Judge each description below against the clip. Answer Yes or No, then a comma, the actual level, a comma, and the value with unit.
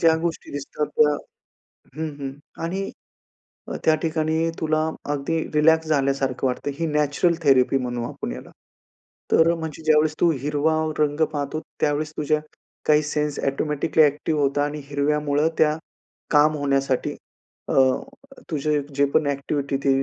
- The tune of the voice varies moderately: No, narrow, 1.8 semitones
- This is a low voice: No, medium, 150 Hz